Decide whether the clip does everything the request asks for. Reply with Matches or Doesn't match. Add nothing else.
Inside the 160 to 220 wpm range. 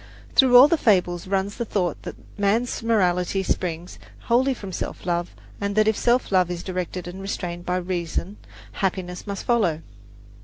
Matches